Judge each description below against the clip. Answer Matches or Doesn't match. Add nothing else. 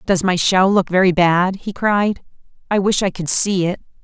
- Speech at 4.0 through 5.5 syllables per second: Matches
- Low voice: Doesn't match